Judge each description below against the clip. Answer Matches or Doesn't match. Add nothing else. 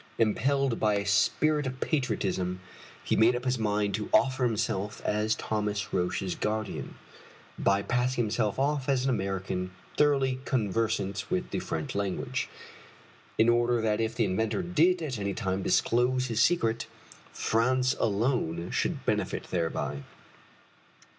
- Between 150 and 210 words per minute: Doesn't match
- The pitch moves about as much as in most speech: Matches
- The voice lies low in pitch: Matches